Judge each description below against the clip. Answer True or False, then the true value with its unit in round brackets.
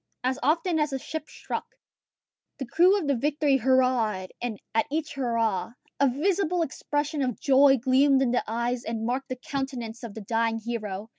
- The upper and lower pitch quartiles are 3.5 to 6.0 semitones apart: True (4.0 semitones)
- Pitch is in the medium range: False (260 Hz)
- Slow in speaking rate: False (175 wpm)